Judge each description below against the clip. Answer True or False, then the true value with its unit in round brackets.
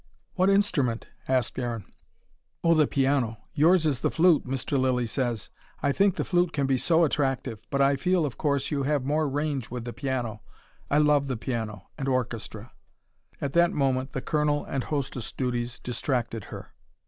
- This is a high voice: False (135 Hz)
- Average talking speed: True (175 wpm)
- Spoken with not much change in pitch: False (3.3 semitones)